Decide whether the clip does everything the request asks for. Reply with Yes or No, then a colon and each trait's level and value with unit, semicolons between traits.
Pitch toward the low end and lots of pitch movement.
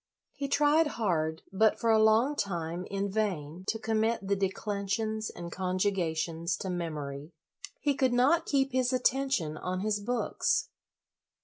No: high, 200 Hz; wide, 5.7 semitones